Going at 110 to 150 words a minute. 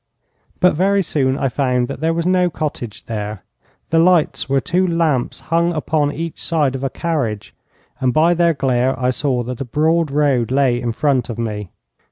No: average, 190 wpm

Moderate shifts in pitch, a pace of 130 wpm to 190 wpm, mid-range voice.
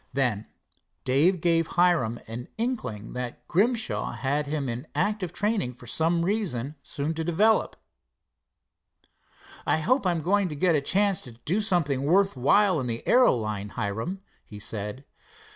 No: wide, 7.5 semitones; average, 150 wpm; medium, 160 Hz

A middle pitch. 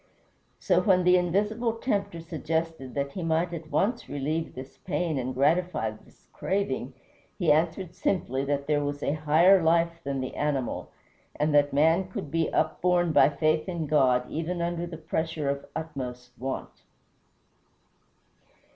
Yes: medium, 160 Hz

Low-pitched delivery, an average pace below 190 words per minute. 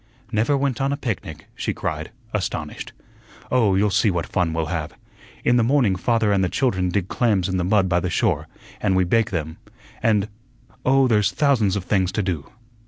No: low, 100 Hz; average, 195 wpm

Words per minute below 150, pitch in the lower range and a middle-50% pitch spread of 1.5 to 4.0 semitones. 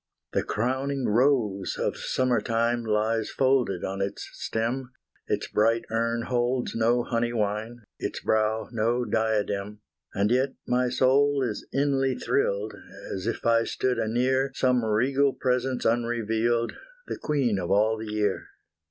Yes: average, 140 wpm; low, 115 Hz; average, 2.9 semitones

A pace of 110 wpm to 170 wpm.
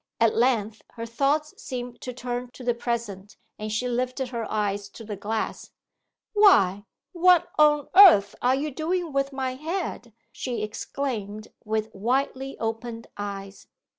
Yes: average, 145 wpm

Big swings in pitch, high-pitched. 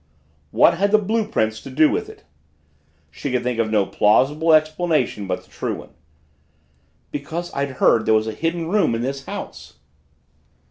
No: wide, 7.0 semitones; medium, 140 Hz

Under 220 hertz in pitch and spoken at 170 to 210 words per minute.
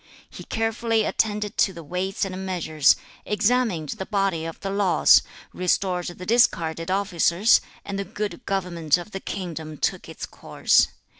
No: high, 190 Hz; average, 155 wpm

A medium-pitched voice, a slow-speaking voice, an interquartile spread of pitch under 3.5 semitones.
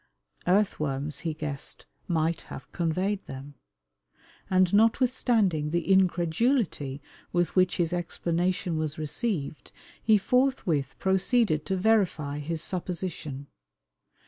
No: medium, 175 Hz; slow, 100 wpm; average, 4.0 semitones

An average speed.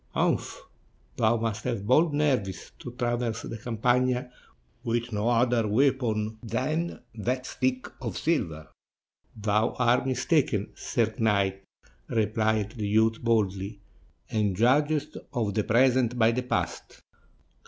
No: slow, 120 wpm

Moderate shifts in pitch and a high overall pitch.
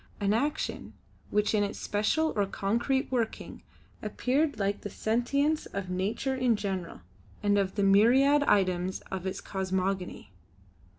Yes: average, 4.9 semitones; high, 205 Hz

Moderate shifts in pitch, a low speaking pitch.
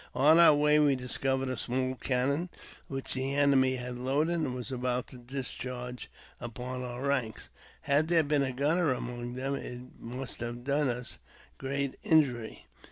No: narrow, 2.2 semitones; low, 130 Hz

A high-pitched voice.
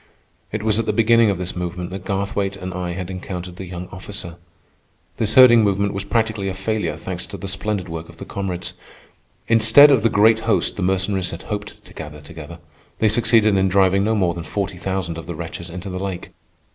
No: very low, 95 Hz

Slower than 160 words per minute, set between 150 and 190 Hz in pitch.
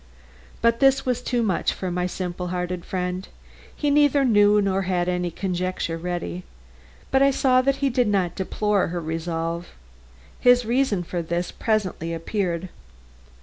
Yes: average, 150 wpm; medium, 185 Hz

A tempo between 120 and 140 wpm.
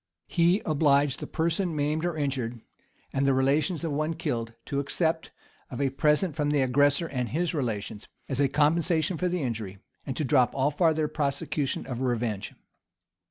No: average, 170 wpm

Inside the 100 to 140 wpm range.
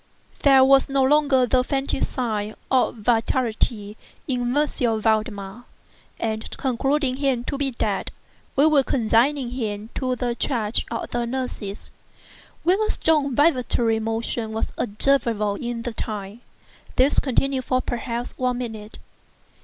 Yes: slow, 135 wpm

